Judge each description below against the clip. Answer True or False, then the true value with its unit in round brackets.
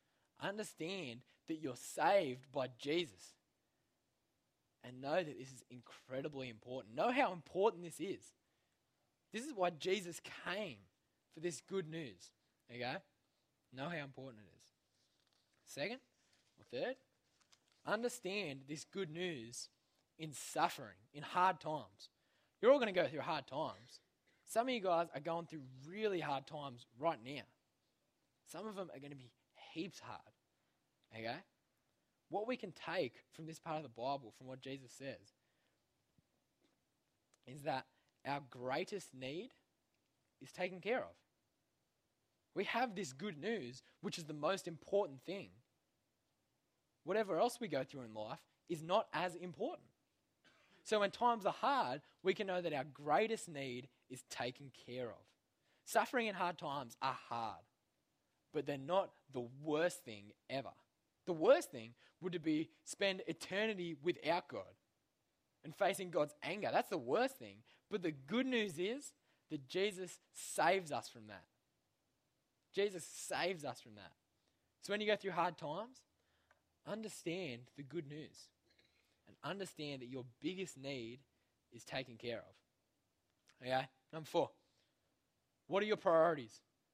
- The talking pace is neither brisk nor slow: True (145 wpm)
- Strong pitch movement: True (6.2 semitones)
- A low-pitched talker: False (155 Hz)